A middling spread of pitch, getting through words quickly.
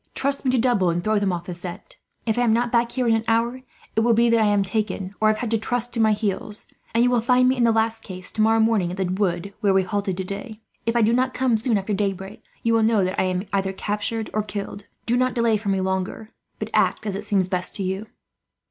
Yes: average, 3.2 semitones; fast, 265 wpm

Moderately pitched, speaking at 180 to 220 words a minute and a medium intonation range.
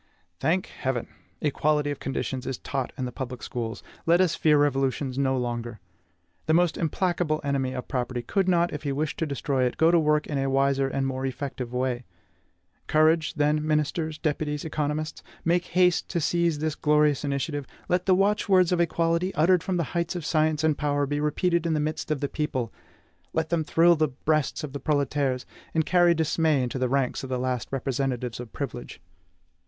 Yes: medium, 150 Hz; average, 190 wpm; average, 3.4 semitones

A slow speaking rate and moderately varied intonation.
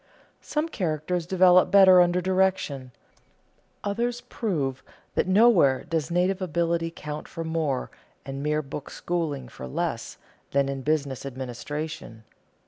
Yes: slow, 125 wpm; average, 5.0 semitones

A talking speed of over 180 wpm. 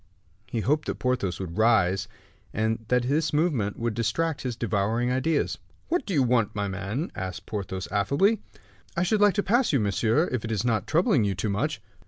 Yes: average, 195 wpm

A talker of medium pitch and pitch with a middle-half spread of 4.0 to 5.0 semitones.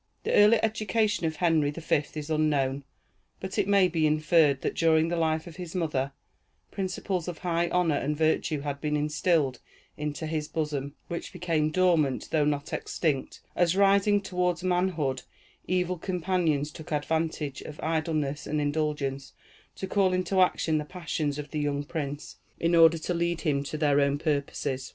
No: medium, 160 Hz; average, 3.3 semitones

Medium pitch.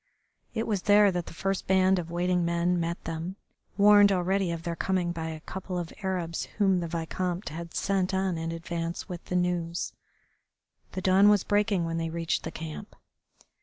Yes: medium, 180 Hz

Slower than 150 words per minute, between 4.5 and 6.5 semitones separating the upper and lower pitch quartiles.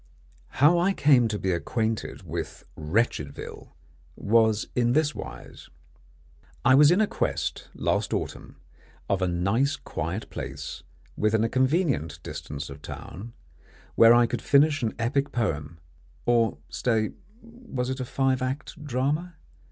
Yes: slow, 135 wpm; average, 5.0 semitones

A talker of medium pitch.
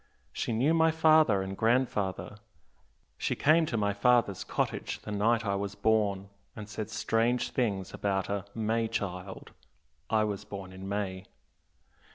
No: low, 105 Hz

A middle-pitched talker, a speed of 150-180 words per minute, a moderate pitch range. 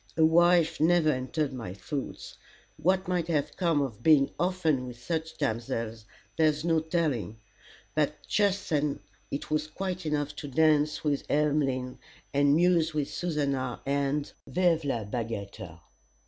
No: medium, 150 Hz; average, 140 wpm; average, 3.8 semitones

